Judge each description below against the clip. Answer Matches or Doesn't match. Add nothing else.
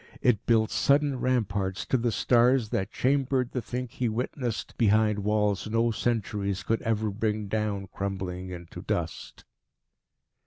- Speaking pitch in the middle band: Doesn't match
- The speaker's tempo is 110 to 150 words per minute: Matches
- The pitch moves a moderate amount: Matches